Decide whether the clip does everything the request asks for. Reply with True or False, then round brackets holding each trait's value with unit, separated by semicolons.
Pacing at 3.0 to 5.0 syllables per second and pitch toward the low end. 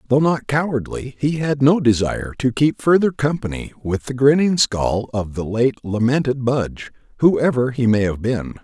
True (4.8 syllables/s; 125 Hz)